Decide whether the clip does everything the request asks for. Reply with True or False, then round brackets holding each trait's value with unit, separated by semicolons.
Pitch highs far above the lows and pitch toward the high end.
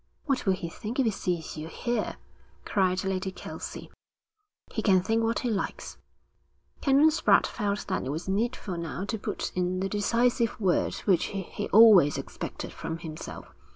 False (4.0 semitones; 195 Hz)